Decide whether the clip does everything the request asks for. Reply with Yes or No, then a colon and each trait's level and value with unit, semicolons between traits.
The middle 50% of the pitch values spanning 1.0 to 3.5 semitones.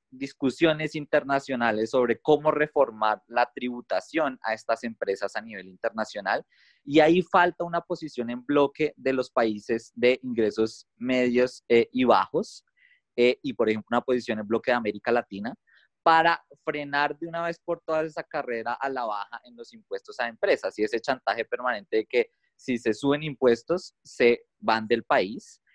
No: wide, 5.6 semitones